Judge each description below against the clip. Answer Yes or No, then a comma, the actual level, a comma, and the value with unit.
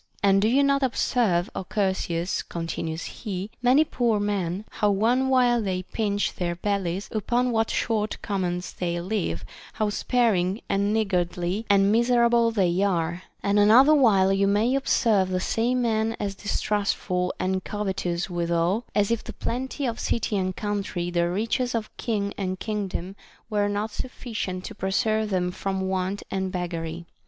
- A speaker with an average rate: Yes, average, 160 wpm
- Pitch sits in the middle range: No, high, 200 Hz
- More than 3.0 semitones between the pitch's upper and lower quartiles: Yes, average, 3.4 semitones